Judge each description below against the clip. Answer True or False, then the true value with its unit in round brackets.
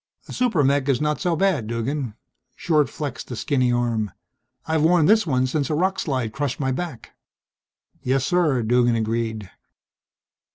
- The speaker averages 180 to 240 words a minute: False (160 wpm)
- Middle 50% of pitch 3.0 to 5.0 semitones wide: True (4.5 semitones)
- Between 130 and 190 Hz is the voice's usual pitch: True (135 Hz)